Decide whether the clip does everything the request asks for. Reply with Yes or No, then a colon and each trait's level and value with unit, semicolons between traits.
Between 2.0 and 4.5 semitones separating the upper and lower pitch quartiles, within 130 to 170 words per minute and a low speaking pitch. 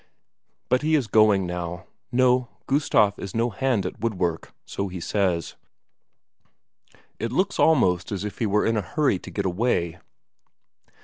No: average, 5.2 semitones; average, 150 wpm; low, 105 Hz